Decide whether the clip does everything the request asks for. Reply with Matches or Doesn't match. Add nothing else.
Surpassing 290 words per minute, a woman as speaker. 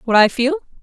Doesn't match